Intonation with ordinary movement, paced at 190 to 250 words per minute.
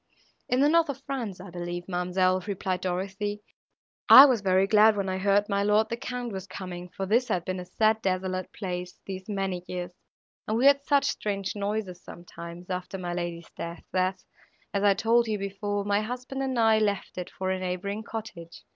Yes: average, 3.1 semitones; average, 195 wpm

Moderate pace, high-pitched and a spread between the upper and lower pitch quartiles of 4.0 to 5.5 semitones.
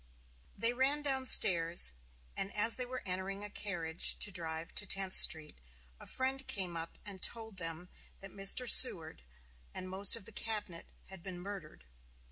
Yes: average, 165 wpm; high, 195 Hz; average, 4.6 semitones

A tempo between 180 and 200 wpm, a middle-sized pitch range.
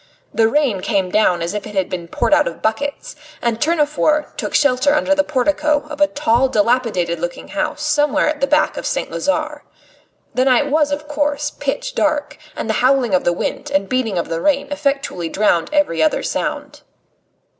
No: average, 190 wpm; wide, 5.9 semitones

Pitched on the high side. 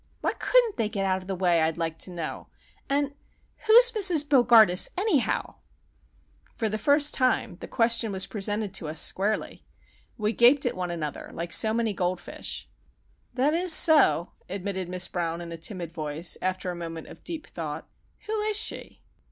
Yes: high, 200 Hz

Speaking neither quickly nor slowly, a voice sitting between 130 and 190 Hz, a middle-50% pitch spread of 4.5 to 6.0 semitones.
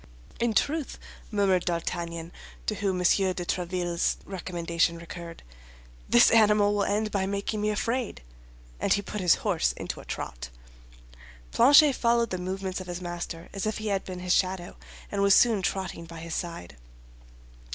No: average, 160 wpm; medium, 185 Hz; average, 3.3 semitones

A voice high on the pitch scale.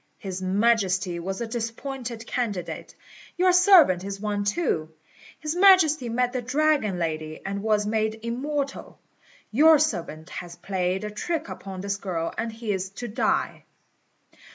Yes: high, 215 Hz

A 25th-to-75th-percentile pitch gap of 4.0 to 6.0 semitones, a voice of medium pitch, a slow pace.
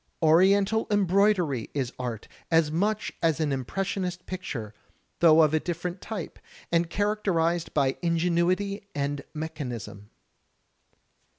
Yes: average, 4.4 semitones; medium, 170 Hz; slow, 110 wpm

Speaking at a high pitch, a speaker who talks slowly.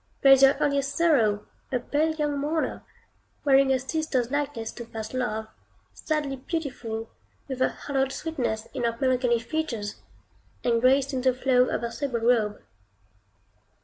No: very high, 260 Hz; average, 150 wpm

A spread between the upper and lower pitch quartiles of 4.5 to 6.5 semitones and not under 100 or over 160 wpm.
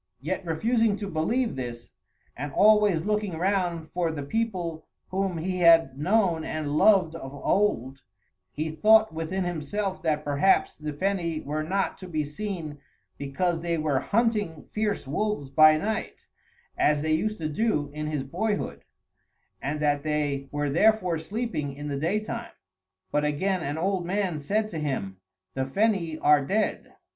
Yes: average, 5.1 semitones; average, 155 wpm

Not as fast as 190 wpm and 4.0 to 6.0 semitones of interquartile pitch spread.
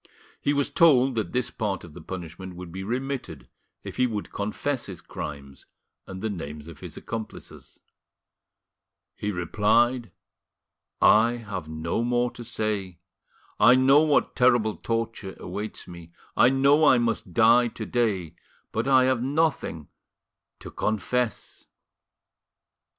Yes: slow, 135 wpm; average, 5.0 semitones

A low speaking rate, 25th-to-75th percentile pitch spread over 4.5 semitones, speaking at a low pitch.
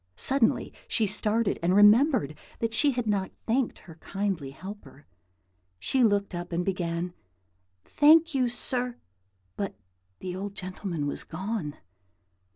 No: slow, 130 wpm; average, 5.1 semitones; high, 200 Hz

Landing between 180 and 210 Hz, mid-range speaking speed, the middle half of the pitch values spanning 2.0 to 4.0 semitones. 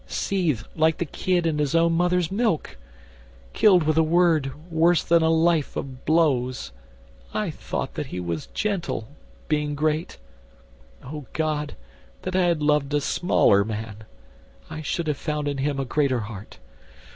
No: medium, 155 Hz; average, 155 wpm; average, 3.6 semitones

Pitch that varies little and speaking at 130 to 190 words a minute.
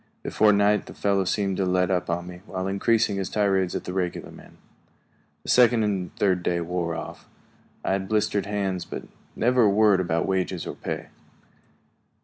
Yes: narrow, 2.3 semitones; average, 180 wpm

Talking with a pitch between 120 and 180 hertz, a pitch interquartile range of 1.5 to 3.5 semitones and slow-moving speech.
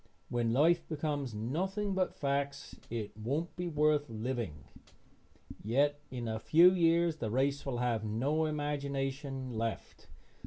No: medium, 140 Hz; average, 4.7 semitones; slow, 130 wpm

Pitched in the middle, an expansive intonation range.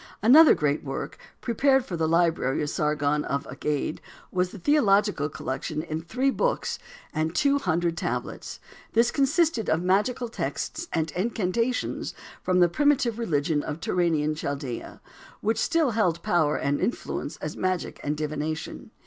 Yes: medium, 175 Hz; wide, 7.5 semitones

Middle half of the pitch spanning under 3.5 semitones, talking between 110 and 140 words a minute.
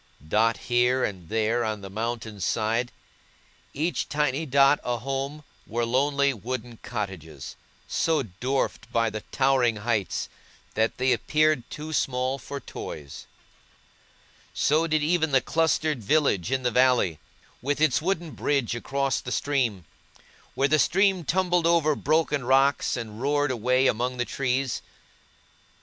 No: average, 4.2 semitones; slow, 135 wpm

